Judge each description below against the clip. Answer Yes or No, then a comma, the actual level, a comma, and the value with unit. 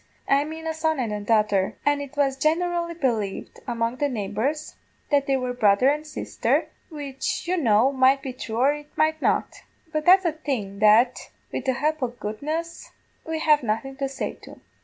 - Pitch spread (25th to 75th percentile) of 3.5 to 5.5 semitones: Yes, average, 4.7 semitones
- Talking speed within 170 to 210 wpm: Yes, average, 185 wpm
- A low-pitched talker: No, very high, 275 Hz